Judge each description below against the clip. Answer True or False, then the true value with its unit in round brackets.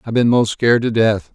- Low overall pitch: True (115 Hz)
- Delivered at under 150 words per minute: False (270 wpm)